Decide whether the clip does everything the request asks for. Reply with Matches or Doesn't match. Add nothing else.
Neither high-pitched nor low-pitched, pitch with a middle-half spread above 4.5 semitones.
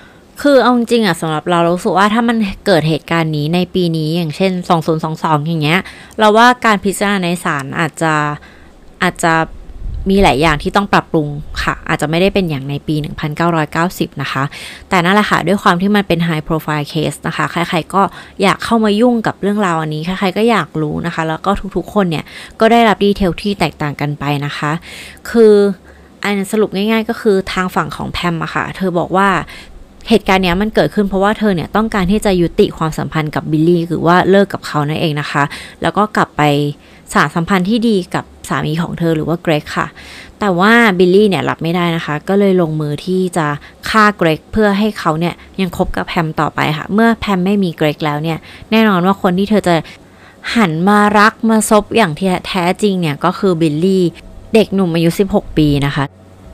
Doesn't match